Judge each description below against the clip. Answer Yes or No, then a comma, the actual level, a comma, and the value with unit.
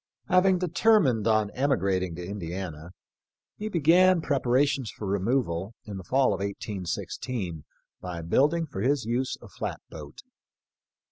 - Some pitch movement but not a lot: No, wide, 7.5 semitones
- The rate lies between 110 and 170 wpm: Yes, slow, 135 wpm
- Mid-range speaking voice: No, low, 115 Hz